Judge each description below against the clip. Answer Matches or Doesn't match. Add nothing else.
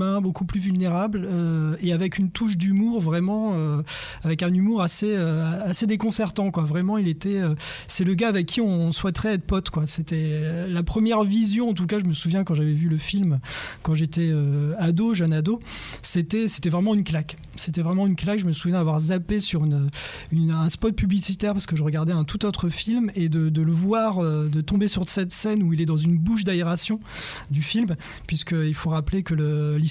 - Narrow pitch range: Doesn't match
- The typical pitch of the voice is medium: Matches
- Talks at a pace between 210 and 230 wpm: Matches